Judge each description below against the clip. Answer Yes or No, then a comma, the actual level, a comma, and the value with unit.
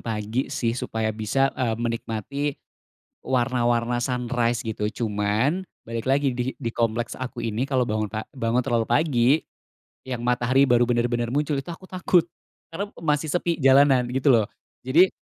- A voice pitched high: No, low, 120 Hz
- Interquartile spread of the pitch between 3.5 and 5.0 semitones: No, average, 2.8 semitones